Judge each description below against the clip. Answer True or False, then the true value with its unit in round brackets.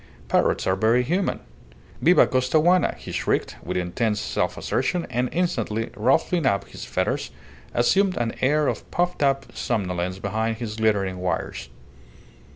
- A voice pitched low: True (115 Hz)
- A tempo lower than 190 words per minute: True (140 wpm)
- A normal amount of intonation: False (7.1 semitones)